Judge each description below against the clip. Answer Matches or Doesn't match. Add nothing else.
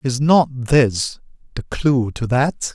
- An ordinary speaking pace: Matches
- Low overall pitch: Matches